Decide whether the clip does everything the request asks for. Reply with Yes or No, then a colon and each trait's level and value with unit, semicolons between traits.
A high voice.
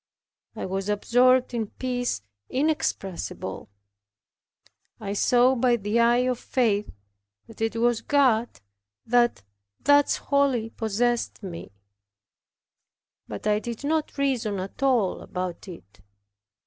Yes: high, 235 Hz